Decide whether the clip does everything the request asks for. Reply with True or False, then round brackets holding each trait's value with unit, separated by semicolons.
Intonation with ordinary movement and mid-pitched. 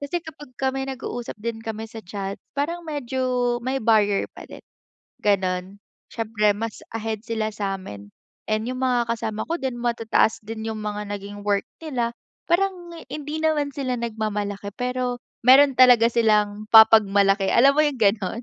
False (3.8 semitones; 230 Hz)